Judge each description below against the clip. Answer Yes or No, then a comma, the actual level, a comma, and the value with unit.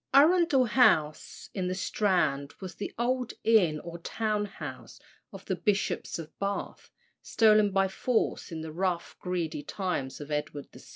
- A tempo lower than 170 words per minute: Yes, average, 155 wpm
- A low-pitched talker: No, high, 190 Hz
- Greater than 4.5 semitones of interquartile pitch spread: Yes, average, 5.2 semitones